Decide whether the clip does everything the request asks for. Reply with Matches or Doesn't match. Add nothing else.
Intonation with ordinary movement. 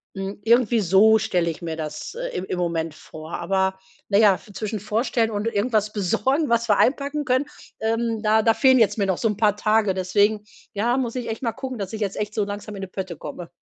Matches